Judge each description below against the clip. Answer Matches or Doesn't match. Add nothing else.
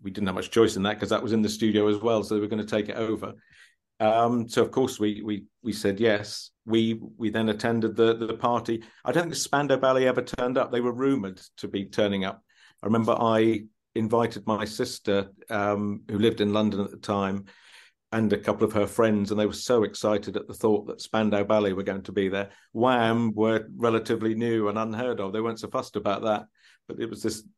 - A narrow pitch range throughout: Matches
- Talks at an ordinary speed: Doesn't match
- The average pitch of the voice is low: Matches